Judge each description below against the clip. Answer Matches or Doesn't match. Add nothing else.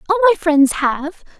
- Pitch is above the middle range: Matches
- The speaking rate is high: Doesn't match